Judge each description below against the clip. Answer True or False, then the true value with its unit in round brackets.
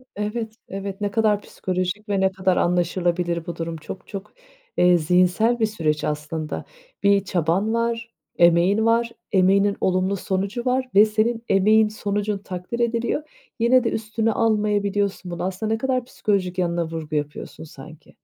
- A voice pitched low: False (200 Hz)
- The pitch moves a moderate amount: True (3.6 semitones)